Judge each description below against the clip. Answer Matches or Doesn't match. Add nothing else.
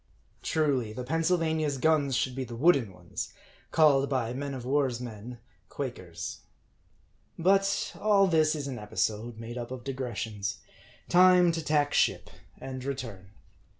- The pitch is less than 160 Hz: Matches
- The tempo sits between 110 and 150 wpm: Matches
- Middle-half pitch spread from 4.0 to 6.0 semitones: Matches